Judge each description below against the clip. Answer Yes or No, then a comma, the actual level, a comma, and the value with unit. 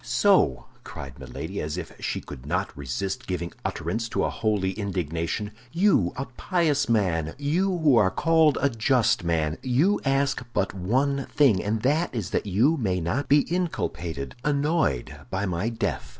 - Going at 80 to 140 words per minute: No, average, 160 wpm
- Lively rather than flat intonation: Yes, wide, 8.2 semitones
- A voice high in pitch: No, low, 110 Hz